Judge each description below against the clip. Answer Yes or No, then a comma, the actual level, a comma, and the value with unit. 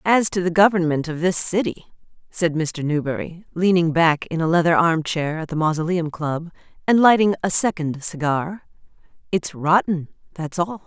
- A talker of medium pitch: Yes, medium, 170 Hz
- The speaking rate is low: No, average, 160 wpm